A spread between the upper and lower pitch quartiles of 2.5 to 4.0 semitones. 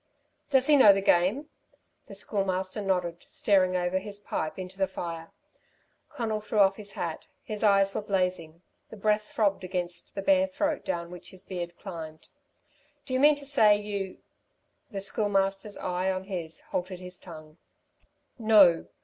Yes: average, 2.9 semitones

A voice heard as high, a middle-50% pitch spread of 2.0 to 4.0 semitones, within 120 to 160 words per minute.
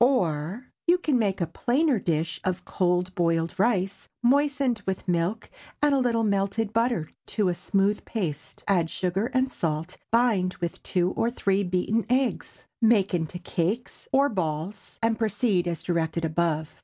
No: high, 195 Hz; average, 5.2 semitones; average, 155 wpm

